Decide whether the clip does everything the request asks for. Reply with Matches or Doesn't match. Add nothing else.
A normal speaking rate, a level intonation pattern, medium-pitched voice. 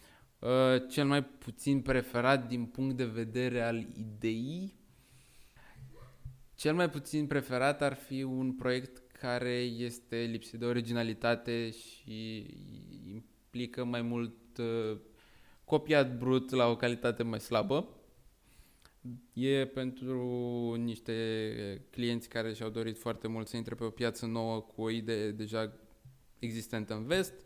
Doesn't match